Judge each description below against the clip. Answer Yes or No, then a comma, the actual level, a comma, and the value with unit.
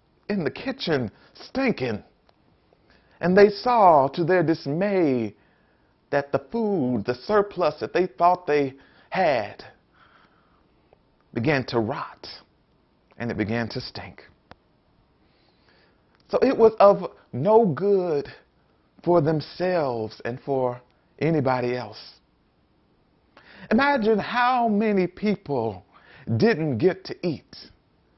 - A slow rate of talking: Yes, slow, 100 wpm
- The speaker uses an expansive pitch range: Yes, wide, 8.2 semitones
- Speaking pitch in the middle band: Yes, medium, 170 Hz